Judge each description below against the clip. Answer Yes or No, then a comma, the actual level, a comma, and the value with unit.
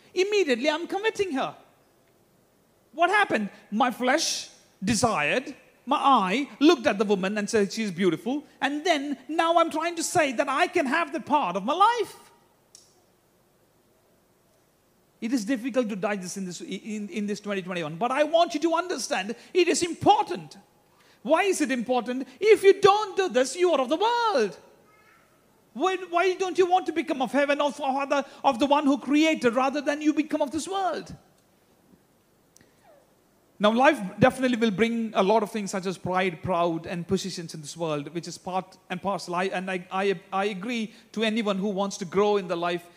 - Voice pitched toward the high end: Yes, very high, 260 Hz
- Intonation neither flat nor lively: No, wide, 8.4 semitones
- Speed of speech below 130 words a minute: No, fast, 180 wpm